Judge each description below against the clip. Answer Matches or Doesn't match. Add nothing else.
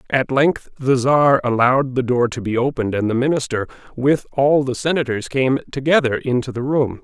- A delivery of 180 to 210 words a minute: Matches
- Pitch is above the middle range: Doesn't match